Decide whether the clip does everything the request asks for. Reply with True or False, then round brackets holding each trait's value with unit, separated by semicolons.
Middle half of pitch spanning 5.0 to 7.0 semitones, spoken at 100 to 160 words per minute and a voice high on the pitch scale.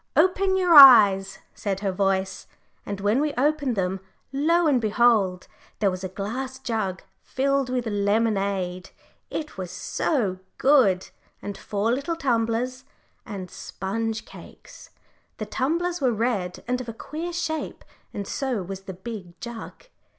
True (5.6 semitones; 145 wpm; 225 Hz)